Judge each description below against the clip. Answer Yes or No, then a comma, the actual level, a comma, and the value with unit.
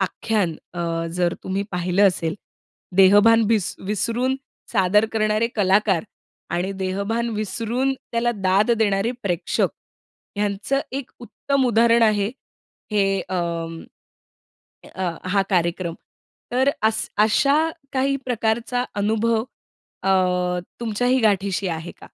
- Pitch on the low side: No, high, 210 Hz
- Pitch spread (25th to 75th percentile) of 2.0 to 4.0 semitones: Yes, average, 3.6 semitones